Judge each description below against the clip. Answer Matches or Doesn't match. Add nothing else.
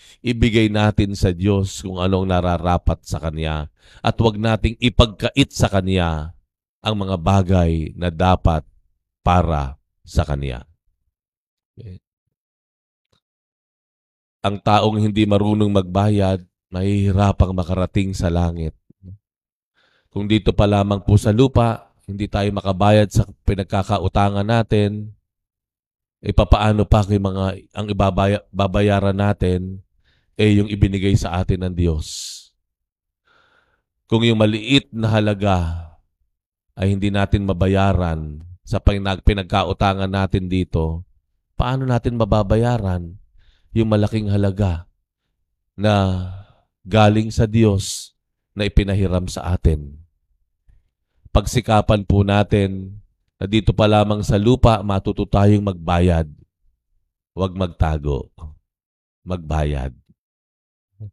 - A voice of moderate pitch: Doesn't match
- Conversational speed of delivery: Doesn't match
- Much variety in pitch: Doesn't match